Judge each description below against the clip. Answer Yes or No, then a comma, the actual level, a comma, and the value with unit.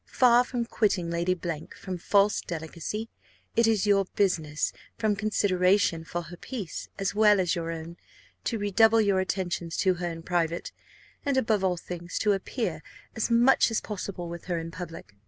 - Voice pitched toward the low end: No, medium, 185 Hz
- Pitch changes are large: No, average, 3.8 semitones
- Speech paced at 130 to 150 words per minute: No, average, 170 wpm